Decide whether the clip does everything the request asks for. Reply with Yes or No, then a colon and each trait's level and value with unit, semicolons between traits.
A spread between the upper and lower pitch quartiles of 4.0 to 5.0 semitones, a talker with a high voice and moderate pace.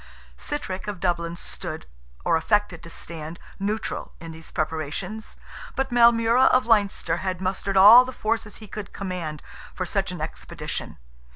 Yes: average, 4.7 semitones; high, 195 Hz; average, 150 wpm